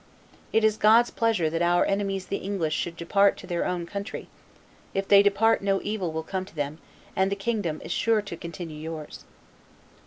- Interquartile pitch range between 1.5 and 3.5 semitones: Yes, average, 3.2 semitones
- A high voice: Yes, high, 195 Hz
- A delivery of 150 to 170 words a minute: No, average, 190 wpm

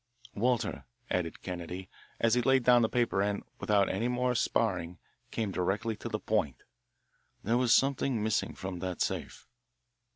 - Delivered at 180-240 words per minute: No, average, 155 wpm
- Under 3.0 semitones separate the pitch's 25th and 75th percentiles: No, average, 4.6 semitones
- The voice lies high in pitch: No, low, 110 Hz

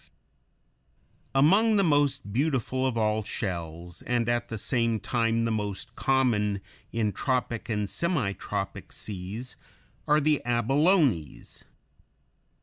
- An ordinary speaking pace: No, slow, 115 wpm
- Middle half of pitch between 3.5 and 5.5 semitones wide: Yes, average, 4.6 semitones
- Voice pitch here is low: Yes, low, 115 Hz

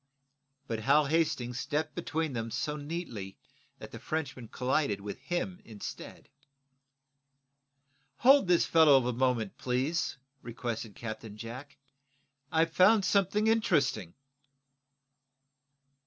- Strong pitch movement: Yes, wide, 5.9 semitones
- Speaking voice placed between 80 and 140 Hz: Yes, low, 135 Hz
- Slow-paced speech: Yes, slow, 105 wpm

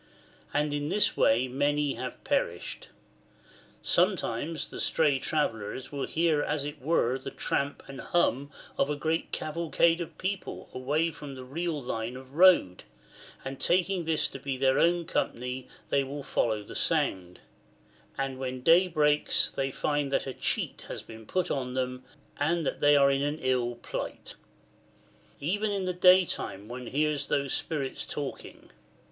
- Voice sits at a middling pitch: Yes, medium, 145 Hz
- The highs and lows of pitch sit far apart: No, average, 3.8 semitones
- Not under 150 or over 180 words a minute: Yes, average, 160 wpm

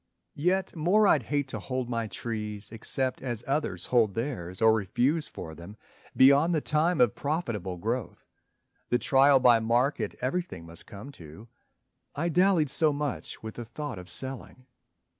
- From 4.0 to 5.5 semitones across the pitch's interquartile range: Yes, average, 5.1 semitones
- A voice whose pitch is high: No, low, 125 Hz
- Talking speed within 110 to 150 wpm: No, average, 160 wpm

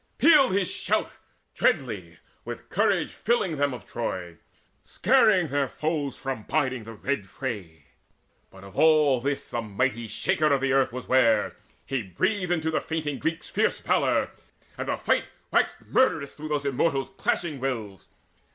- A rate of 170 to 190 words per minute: No, average, 150 wpm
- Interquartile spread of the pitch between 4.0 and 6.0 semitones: Yes, average, 5.2 semitones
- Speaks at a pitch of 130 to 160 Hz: Yes, low, 135 Hz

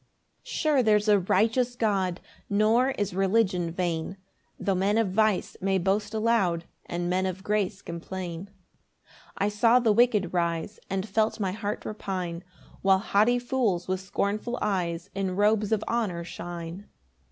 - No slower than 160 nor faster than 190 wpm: No, average, 150 wpm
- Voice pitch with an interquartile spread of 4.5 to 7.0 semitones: No, average, 3.0 semitones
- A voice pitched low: No, high, 200 Hz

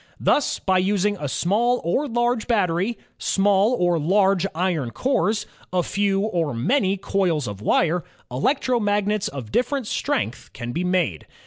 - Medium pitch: No, high, 195 Hz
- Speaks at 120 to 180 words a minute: Yes, average, 140 wpm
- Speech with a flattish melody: No, average, 4.3 semitones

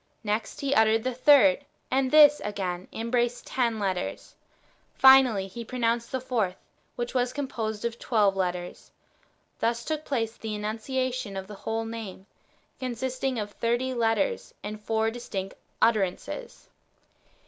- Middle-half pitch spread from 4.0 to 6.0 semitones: No, average, 3.5 semitones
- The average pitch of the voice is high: Yes, high, 230 Hz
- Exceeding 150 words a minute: No, slow, 135 wpm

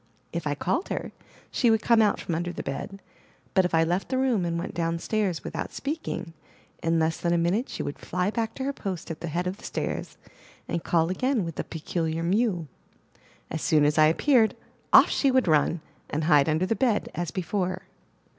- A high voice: No, medium, 175 Hz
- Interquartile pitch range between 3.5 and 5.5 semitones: Yes, average, 4.9 semitones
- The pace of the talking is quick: Yes, fast, 210 wpm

